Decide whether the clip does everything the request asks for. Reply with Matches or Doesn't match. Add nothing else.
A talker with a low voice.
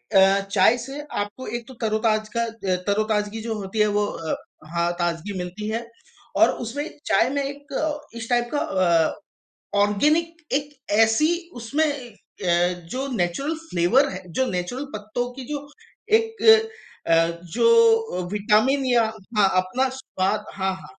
Doesn't match